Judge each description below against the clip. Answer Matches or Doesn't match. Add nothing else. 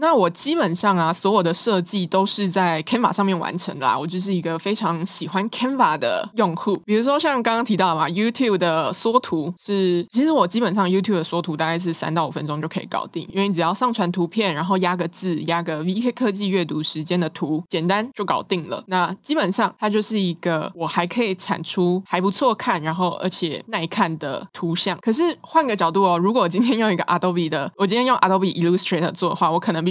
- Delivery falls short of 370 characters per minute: Doesn't match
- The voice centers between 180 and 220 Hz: Matches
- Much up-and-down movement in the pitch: Doesn't match